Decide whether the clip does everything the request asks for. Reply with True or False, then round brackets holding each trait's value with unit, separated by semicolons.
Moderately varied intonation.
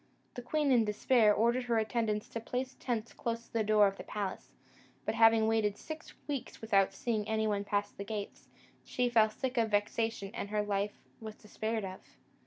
False (2.1 semitones)